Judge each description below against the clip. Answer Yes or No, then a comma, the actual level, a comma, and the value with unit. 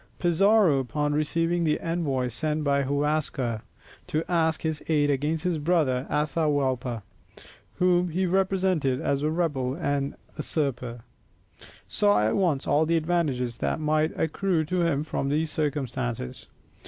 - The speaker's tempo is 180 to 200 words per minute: No, slow, 135 wpm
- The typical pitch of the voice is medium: Yes, medium, 150 Hz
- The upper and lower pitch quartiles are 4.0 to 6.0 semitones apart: No, average, 3.4 semitones